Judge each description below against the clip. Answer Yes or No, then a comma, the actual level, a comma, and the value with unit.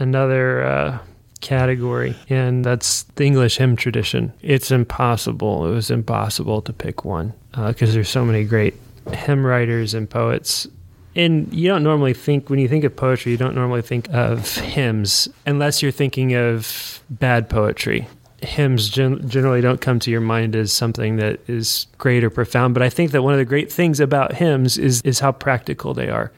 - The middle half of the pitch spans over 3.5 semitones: No, average, 2.9 semitones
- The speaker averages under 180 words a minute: No, average, 185 wpm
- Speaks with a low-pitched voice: Yes, low, 125 Hz